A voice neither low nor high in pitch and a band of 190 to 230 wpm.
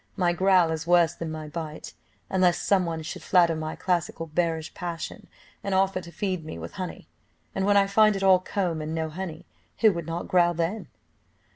Yes: medium, 175 Hz; average, 195 wpm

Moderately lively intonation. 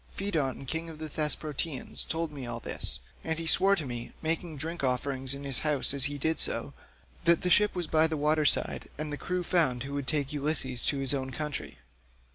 Yes: average, 3.0 semitones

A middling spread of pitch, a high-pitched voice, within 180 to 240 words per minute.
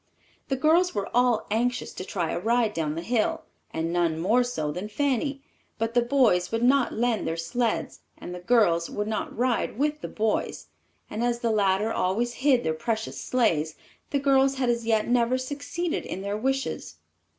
Yes: average, 5.0 semitones; high, 230 Hz; average, 185 wpm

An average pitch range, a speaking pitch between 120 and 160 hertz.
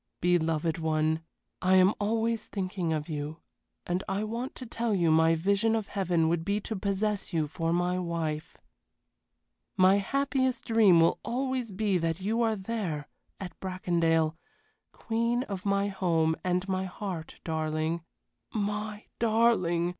No: average, 4.5 semitones; medium, 185 Hz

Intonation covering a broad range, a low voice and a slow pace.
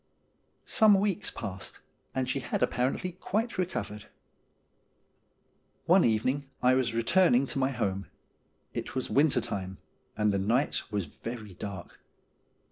Yes: wide, 6.2 semitones; low, 125 Hz; slow, 125 wpm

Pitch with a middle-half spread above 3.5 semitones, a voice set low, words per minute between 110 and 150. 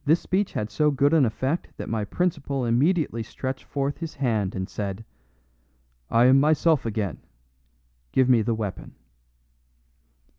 Yes: average, 5.2 semitones; low, 130 Hz; average, 145 wpm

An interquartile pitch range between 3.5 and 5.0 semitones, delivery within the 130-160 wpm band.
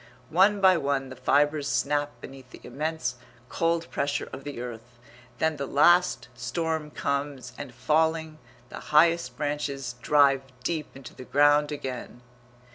No: average, 3.1 semitones; average, 140 wpm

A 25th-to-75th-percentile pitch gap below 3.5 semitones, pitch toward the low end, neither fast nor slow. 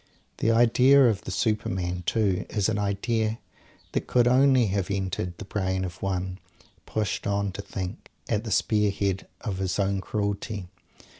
Yes: average, 2.7 semitones; low, 100 Hz; average, 160 wpm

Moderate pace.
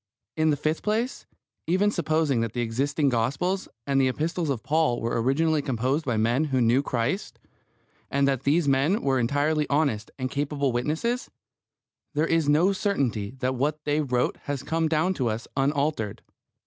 Yes: average, 170 wpm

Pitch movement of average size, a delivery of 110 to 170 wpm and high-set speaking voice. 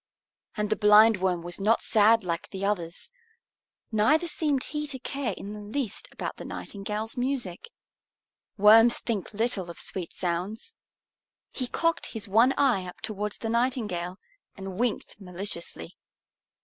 Yes: average, 4.0 semitones; average, 140 wpm; high, 210 Hz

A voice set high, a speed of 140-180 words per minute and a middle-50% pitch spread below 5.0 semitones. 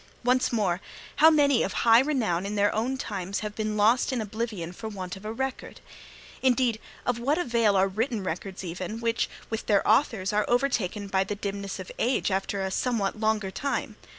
No: high, 215 Hz; average, 190 wpm; average, 3.7 semitones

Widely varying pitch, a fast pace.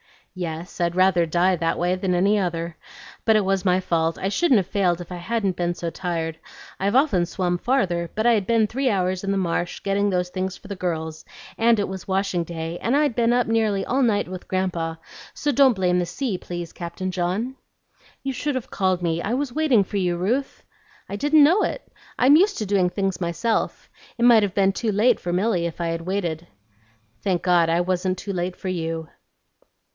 No: average, 4.0 semitones; fast, 210 wpm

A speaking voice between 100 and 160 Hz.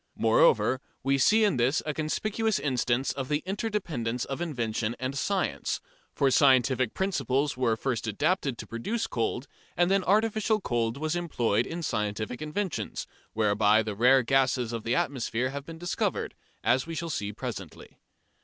Yes: low, 135 Hz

